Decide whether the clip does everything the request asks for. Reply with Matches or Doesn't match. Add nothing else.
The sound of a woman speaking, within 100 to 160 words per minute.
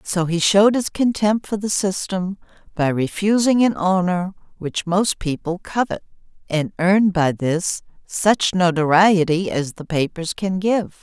Matches